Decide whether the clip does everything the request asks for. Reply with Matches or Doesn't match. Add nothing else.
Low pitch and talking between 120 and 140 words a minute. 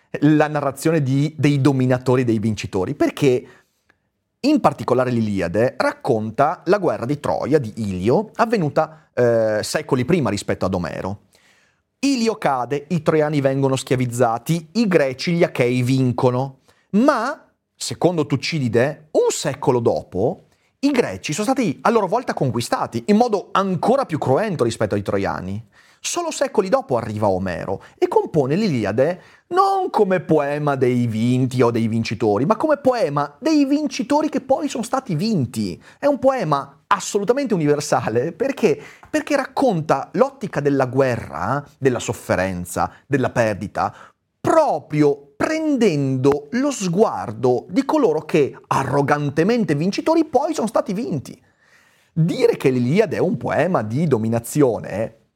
Doesn't match